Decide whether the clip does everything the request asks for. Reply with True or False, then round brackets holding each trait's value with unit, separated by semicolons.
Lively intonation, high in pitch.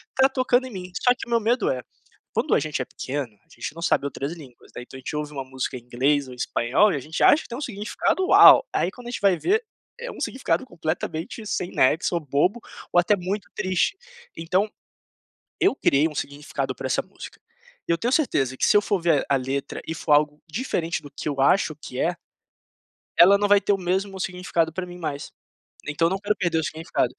False (6.1 semitones; 170 Hz)